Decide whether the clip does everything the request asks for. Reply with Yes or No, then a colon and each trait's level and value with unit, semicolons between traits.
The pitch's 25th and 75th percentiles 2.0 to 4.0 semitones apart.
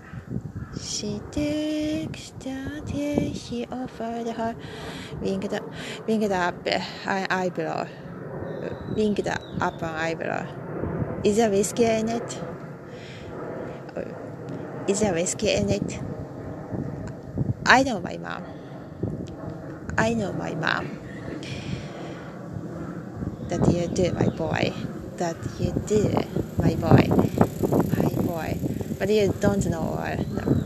No: average, 5.3 semitones